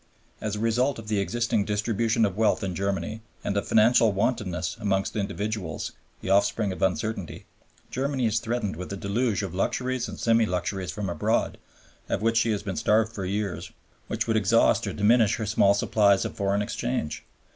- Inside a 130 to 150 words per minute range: No, average, 180 wpm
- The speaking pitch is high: No, low, 105 Hz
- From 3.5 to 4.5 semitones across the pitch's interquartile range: No, narrow, 2.5 semitones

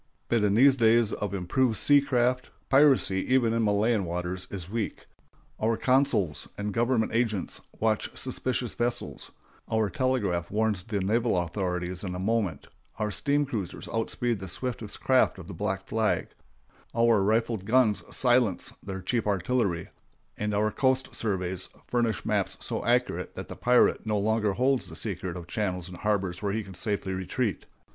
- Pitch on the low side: Yes, low, 110 Hz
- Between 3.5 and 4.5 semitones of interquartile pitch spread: Yes, average, 4.0 semitones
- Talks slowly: No, average, 160 wpm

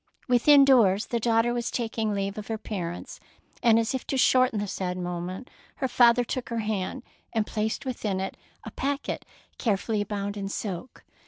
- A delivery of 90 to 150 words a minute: No, average, 180 wpm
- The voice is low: No, high, 220 Hz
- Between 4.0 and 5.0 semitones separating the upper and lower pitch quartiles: No, average, 3.5 semitones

